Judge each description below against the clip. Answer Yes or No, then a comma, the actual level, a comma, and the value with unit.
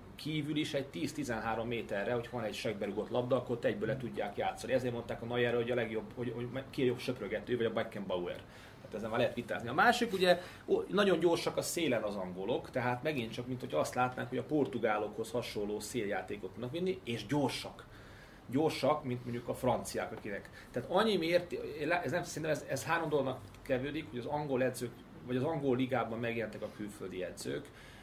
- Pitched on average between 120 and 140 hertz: Yes, low, 125 Hz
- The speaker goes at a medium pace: No, fast, 190 wpm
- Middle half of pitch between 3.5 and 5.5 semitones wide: Yes, average, 4.4 semitones